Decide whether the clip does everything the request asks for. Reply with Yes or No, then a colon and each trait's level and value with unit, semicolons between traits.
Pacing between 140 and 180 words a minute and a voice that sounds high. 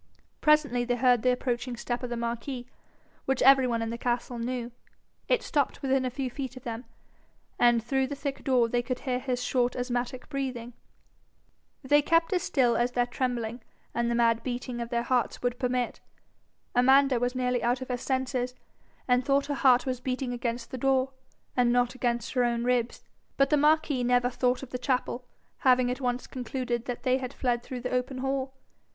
No: average, 195 wpm; very high, 250 Hz